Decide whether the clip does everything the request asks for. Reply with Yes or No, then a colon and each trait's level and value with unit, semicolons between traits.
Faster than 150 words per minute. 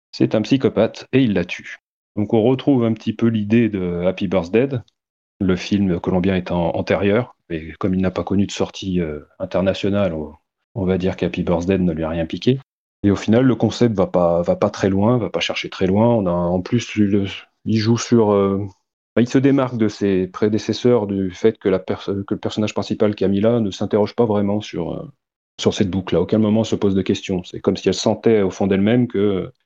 Yes: fast, 220 wpm